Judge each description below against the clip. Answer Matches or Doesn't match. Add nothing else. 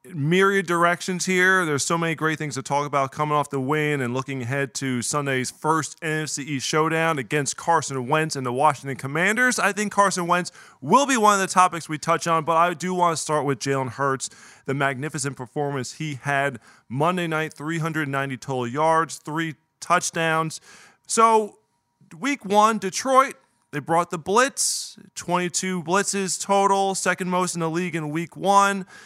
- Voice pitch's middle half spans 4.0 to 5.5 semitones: Matches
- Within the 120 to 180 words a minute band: Matches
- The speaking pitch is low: Doesn't match